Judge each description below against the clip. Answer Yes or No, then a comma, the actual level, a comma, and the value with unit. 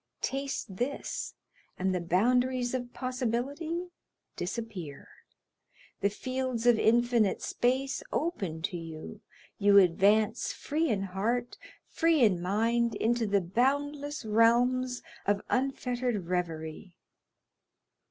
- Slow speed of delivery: Yes, slow, 105 wpm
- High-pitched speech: Yes, high, 235 Hz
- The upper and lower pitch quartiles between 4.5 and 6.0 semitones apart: Yes, average, 4.8 semitones